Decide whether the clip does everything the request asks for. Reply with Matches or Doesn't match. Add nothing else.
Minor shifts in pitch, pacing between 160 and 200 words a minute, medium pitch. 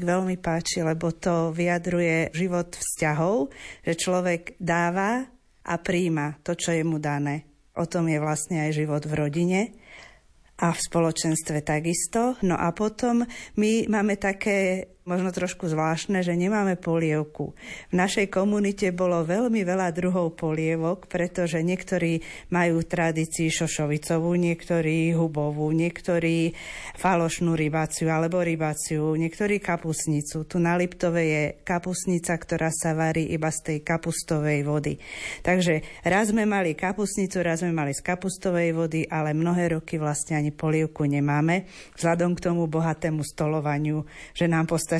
Doesn't match